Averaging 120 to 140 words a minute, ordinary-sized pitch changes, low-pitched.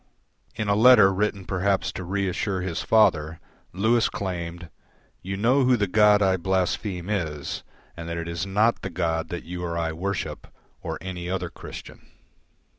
No: average, 165 wpm; average, 3.1 semitones; very low, 95 Hz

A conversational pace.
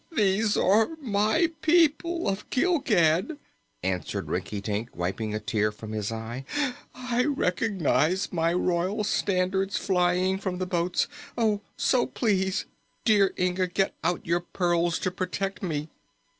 No: slow, 125 wpm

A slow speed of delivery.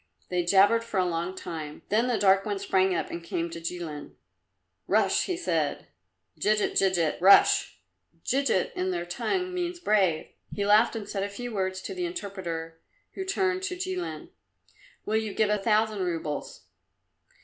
No: average, 165 wpm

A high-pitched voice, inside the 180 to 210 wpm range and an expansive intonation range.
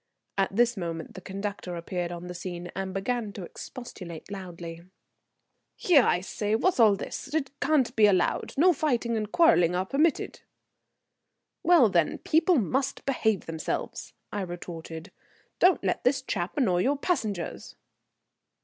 No: high, 205 Hz; average, 145 wpm; wide, 6.7 semitones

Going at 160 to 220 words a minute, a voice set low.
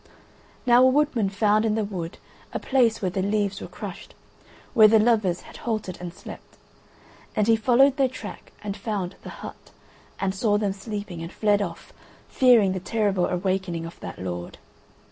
No: average, 175 wpm; high, 205 Hz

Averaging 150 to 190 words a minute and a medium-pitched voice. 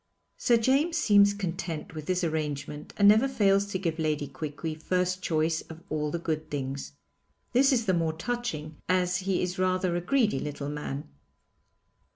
Yes: average, 170 wpm; medium, 175 Hz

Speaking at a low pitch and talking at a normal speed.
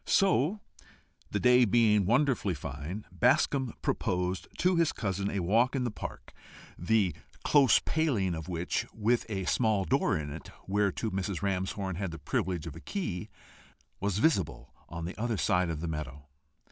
Yes: low, 100 Hz; average, 160 wpm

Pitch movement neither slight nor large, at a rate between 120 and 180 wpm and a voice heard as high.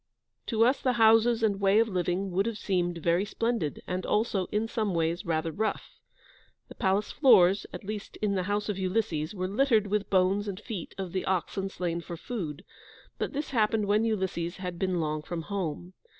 No: average, 3.5 semitones; average, 195 wpm; high, 195 Hz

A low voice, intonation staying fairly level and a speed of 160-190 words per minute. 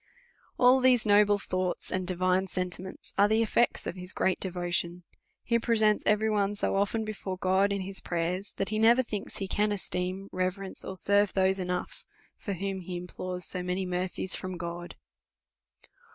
No: high, 190 Hz; narrow, 2.2 semitones; average, 180 wpm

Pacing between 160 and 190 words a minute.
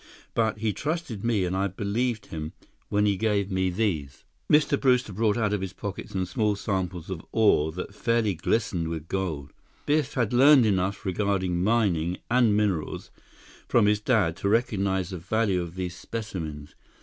Yes: average, 165 wpm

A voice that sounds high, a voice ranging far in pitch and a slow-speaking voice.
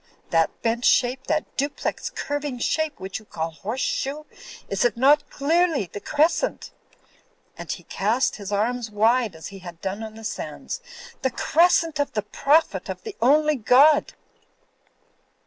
No: very high, 250 Hz; wide, 6.0 semitones; average, 155 wpm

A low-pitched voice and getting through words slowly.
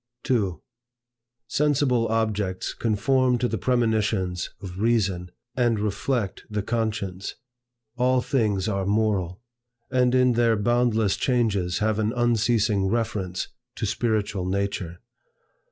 Yes: low, 110 Hz; slow, 110 wpm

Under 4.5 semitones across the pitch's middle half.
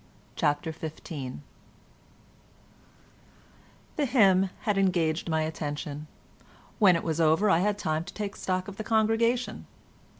No: average, 4.9 semitones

